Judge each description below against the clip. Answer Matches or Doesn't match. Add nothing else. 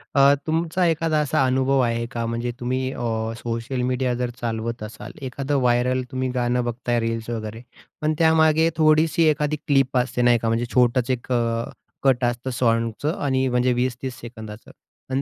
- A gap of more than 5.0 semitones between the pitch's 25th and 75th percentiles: Doesn't match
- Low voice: Matches